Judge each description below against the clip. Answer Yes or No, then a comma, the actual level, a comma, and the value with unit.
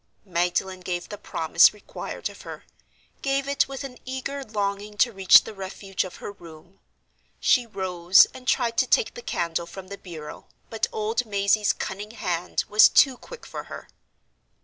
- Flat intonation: No, average, 4.4 semitones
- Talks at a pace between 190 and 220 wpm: No, average, 165 wpm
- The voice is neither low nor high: No, high, 200 Hz